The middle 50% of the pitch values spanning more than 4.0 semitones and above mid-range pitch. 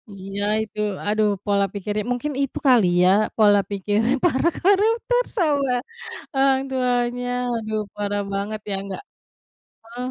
Yes: average, 4.5 semitones; high, 225 Hz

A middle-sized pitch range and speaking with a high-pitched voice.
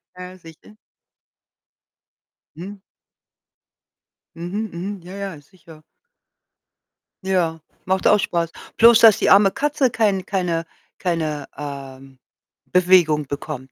No: average, 4.0 semitones; medium, 180 Hz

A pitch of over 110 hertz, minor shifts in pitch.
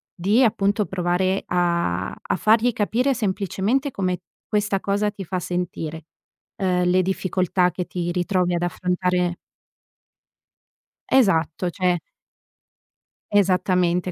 Yes: medium, 185 Hz; narrow, 2.3 semitones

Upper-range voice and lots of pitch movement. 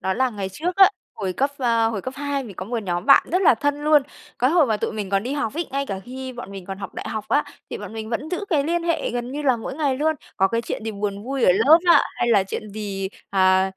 Yes: high, 240 Hz; wide, 6.1 semitones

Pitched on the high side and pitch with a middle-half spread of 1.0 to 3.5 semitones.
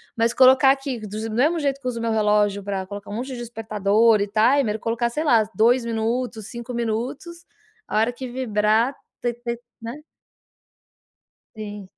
Yes: high, 230 Hz; average, 2.9 semitones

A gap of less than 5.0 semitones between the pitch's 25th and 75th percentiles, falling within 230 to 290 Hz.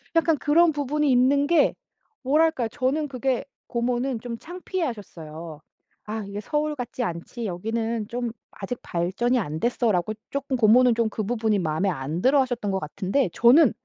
No: average, 5.3 semitones; high, 240 Hz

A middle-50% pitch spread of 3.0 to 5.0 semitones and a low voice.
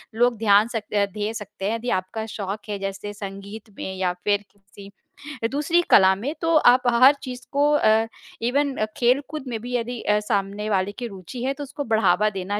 No: average, 3.7 semitones; high, 220 Hz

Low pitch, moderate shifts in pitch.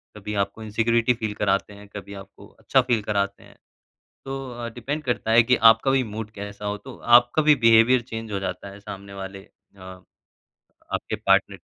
Yes: low, 110 Hz; average, 3.2 semitones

